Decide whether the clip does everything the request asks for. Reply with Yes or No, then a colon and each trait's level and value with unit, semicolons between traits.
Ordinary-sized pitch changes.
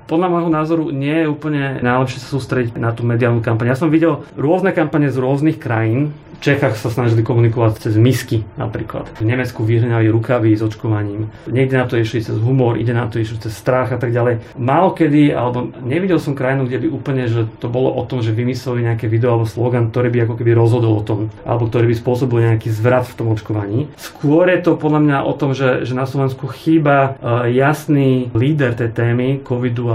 Yes: average, 3.2 semitones